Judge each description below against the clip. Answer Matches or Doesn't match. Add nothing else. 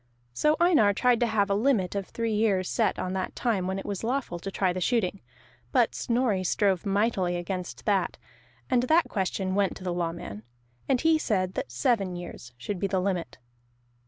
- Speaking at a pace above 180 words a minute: Matches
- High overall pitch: Matches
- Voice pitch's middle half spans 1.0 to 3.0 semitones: Doesn't match